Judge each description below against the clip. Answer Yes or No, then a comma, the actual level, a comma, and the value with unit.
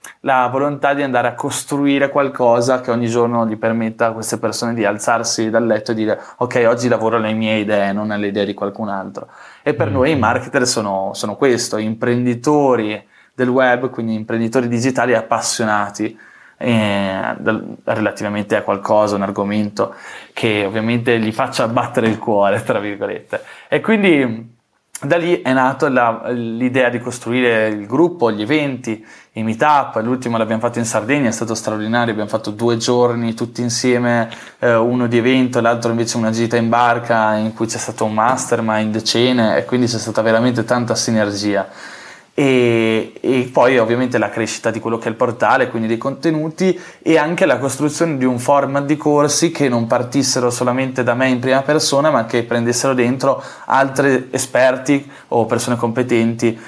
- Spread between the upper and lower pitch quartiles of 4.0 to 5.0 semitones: No, narrow, 2.5 semitones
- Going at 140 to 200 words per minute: Yes, fast, 170 wpm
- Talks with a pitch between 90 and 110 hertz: No, low, 120 Hz